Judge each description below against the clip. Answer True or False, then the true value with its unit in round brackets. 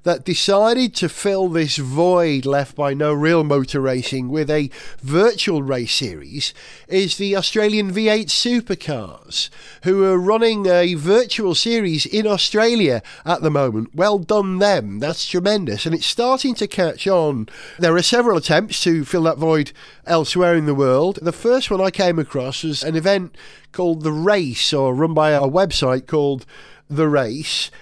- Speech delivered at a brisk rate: False (165 wpm)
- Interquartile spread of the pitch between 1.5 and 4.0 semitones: False (5.0 semitones)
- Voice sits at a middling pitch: True (170 Hz)